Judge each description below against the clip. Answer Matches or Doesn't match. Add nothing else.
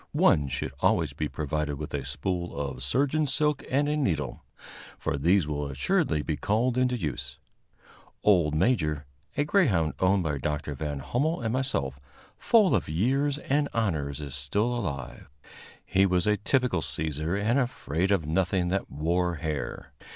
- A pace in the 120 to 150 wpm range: Doesn't match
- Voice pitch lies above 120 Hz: Doesn't match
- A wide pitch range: Matches